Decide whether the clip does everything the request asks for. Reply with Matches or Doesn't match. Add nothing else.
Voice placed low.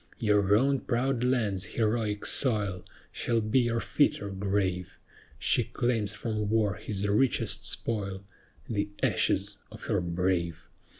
Matches